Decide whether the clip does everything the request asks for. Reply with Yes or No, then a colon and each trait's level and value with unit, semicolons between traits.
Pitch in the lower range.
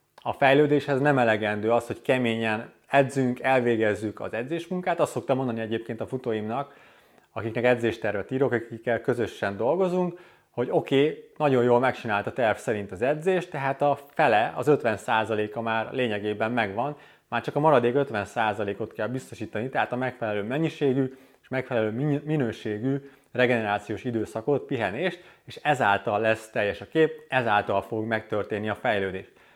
Yes: low, 120 Hz